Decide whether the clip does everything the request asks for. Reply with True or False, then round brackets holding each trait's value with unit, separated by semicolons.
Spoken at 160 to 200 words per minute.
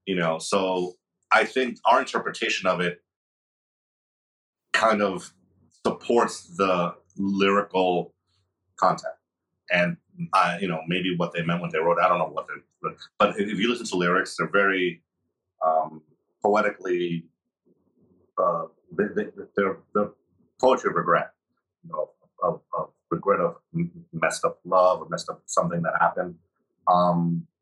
False (140 wpm)